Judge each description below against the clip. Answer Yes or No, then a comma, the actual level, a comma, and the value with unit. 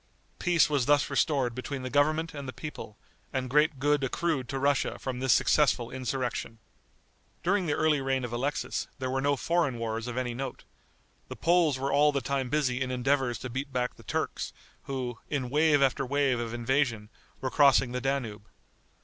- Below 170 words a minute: No, average, 185 wpm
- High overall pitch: No, low, 135 Hz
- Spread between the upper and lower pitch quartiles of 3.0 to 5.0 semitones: No, narrow, 2.6 semitones